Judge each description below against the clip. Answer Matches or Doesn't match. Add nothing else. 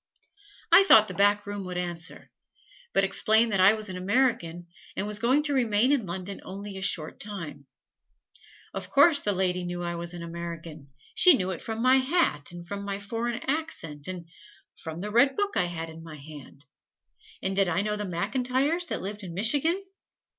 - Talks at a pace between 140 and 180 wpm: Doesn't match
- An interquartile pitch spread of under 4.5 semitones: Doesn't match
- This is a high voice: Matches